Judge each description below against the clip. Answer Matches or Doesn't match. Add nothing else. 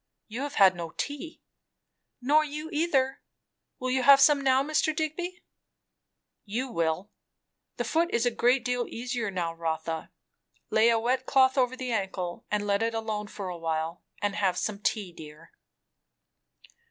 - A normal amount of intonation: Doesn't match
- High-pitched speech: Matches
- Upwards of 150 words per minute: Matches